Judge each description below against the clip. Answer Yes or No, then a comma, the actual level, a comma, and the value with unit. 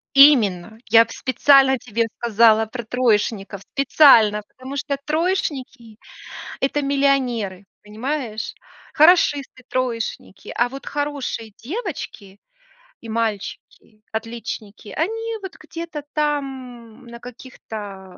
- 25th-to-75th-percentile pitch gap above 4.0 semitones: Yes, average, 4.4 semitones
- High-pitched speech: Yes, high, 245 Hz